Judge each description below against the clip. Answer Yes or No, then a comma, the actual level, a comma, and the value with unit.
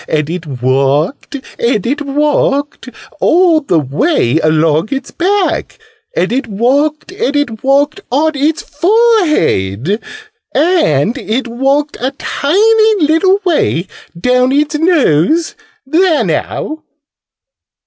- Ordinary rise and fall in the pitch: No, wide, 8.3 semitones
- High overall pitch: Yes, very high, 280 Hz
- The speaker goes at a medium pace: No, slow, 110 wpm